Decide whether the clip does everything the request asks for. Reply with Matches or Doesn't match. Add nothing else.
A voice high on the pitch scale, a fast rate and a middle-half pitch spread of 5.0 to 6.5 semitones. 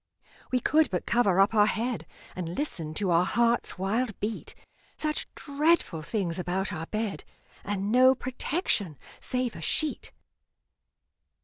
Doesn't match